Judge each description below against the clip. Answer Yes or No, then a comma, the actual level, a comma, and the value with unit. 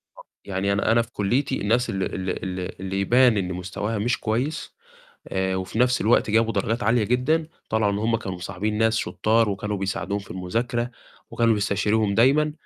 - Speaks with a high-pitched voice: No, low, 110 Hz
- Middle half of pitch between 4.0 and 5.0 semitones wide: No, average, 3.2 semitones